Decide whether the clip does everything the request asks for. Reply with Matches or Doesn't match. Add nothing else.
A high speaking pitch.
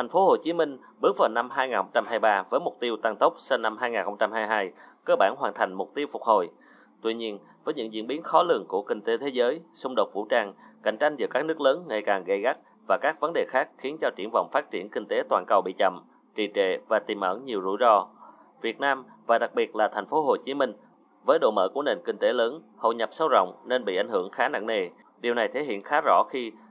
Doesn't match